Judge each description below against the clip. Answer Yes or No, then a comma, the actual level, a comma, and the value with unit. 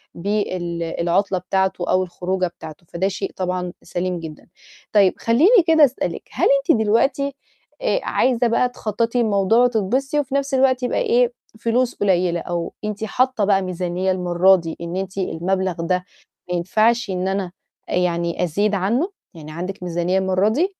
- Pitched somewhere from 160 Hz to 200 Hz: Yes, high, 190 Hz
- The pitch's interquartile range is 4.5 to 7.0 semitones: Yes, average, 4.8 semitones